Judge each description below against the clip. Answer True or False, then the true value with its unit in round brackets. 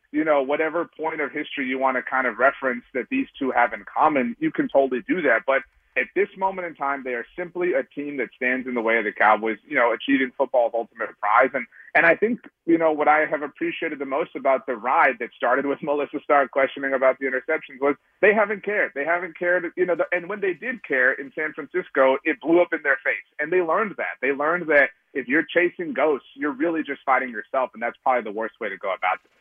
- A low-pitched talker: False (150 Hz)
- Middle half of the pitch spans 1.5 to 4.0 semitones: False (4.9 semitones)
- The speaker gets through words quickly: True (250 wpm)